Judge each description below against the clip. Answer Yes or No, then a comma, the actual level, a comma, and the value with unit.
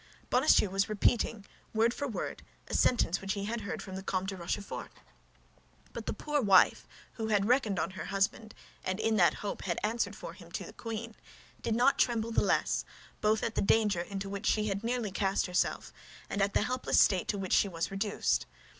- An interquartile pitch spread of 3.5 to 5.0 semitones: No, narrow, 2.6 semitones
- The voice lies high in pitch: Yes, high, 205 Hz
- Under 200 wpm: No, fast, 205 wpm